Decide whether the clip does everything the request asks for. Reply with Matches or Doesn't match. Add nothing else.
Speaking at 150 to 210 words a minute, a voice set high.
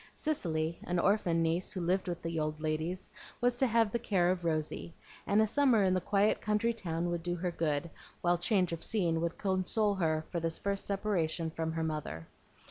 Doesn't match